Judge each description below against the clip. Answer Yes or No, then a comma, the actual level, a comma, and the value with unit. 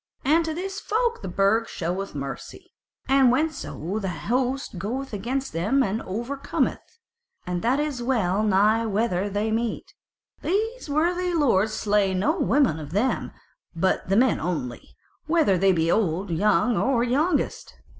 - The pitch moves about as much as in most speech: No, wide, 6.4 semitones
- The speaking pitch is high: Yes, high, 225 Hz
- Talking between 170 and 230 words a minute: No, average, 155 wpm